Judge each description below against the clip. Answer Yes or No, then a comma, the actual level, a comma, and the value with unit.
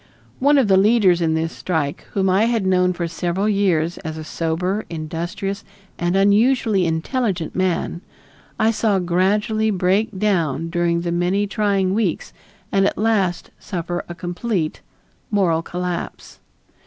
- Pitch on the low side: No, medium, 185 Hz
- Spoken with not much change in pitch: No, average, 3.2 semitones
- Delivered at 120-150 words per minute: Yes, average, 140 wpm